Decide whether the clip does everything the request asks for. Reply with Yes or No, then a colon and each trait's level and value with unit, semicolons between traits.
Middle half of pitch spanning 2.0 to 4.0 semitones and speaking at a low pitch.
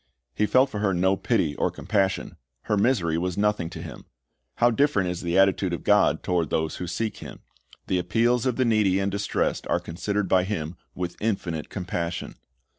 Yes: average, 3.3 semitones; very low, 95 Hz